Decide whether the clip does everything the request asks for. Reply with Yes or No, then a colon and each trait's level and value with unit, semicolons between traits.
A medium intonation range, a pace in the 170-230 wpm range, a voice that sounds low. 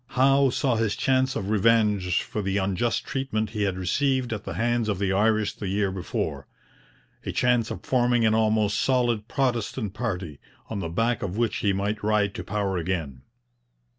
Yes: average, 3.5 semitones; average, 180 wpm; low, 110 Hz